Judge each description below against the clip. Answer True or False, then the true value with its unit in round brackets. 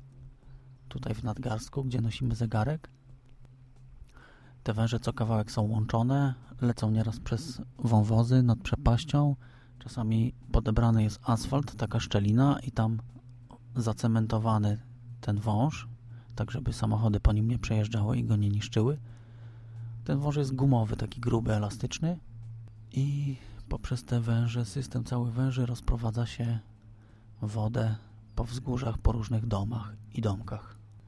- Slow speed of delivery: True (125 wpm)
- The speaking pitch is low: True (115 Hz)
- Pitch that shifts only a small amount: True (2.2 semitones)